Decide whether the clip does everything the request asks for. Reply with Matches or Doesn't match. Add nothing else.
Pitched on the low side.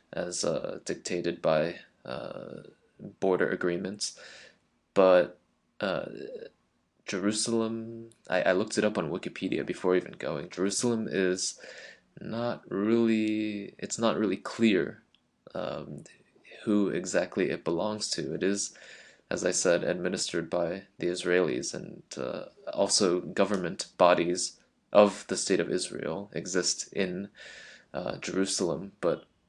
Matches